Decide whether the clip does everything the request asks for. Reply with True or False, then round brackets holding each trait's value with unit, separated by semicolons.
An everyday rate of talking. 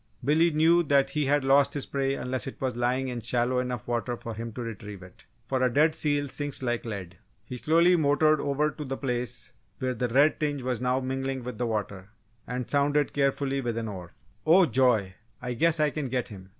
False (215 wpm)